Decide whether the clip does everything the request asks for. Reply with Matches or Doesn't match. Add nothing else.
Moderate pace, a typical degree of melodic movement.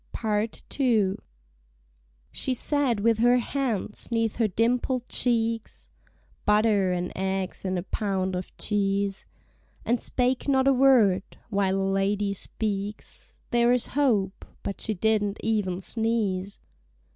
Doesn't match